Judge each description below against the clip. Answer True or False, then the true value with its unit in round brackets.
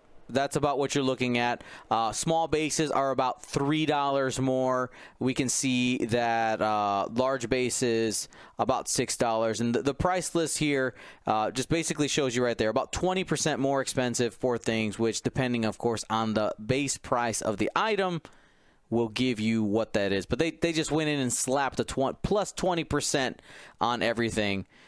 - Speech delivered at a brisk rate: False (180 wpm)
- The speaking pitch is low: True (130 Hz)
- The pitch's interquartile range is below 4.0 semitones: False (4.3 semitones)